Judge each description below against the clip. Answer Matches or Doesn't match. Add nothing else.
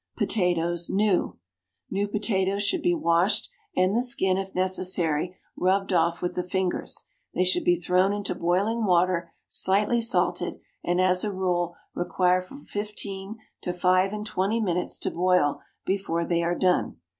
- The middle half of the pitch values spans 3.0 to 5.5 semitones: Doesn't match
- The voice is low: Doesn't match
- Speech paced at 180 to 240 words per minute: Doesn't match